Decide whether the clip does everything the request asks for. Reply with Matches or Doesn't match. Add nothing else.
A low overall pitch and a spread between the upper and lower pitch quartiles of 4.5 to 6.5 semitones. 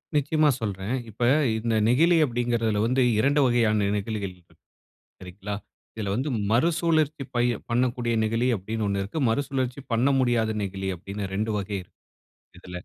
Doesn't match